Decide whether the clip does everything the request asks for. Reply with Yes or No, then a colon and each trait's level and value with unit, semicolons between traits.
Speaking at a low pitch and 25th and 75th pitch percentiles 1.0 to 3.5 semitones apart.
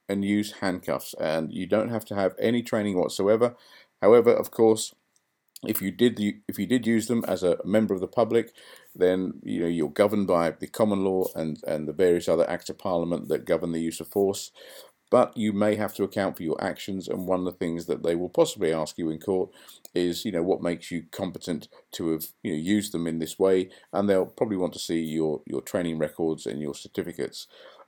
No: very low, 95 Hz; average, 4.0 semitones